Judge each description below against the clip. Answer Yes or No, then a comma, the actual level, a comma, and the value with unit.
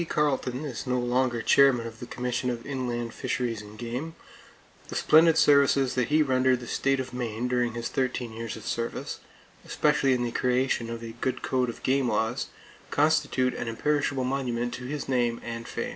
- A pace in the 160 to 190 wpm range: Yes, average, 185 wpm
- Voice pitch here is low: Yes, low, 125 Hz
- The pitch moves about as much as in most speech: No, narrow, 2.3 semitones